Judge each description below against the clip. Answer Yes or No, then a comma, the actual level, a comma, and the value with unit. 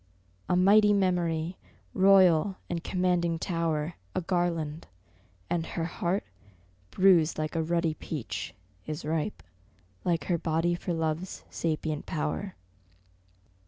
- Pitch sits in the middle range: Yes, medium, 170 Hz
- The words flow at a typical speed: No, slow, 115 wpm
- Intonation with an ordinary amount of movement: No, narrow, 2.3 semitones